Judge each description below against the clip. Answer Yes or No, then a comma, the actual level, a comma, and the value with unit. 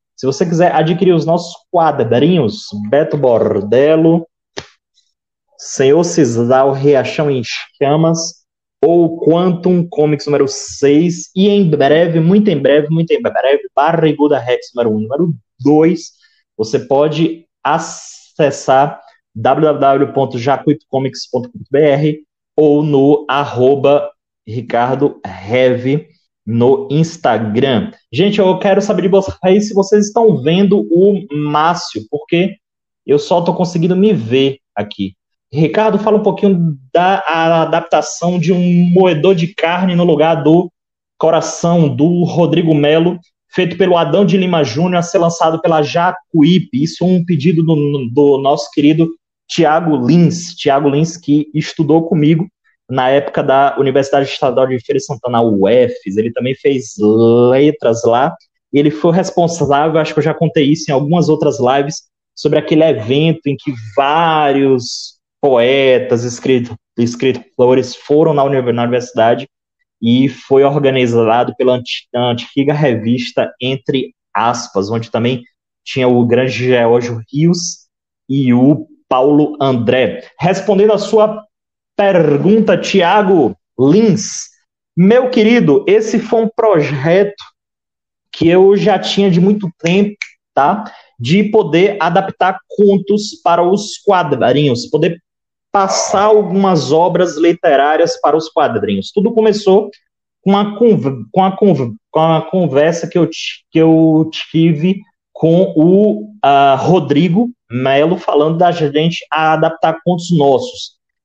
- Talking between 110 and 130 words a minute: Yes, average, 125 wpm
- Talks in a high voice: No, medium, 160 Hz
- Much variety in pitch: No, average, 5.0 semitones